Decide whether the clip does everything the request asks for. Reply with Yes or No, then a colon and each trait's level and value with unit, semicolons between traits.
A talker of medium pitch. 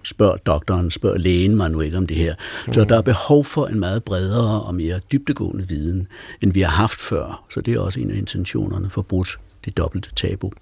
No: very low, 95 Hz